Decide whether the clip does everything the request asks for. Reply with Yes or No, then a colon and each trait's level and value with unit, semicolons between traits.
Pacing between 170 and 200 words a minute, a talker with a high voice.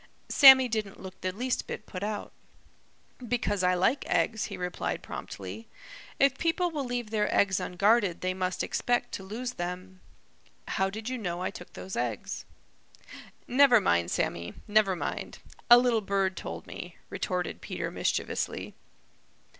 No: average, 150 wpm; high, 205 Hz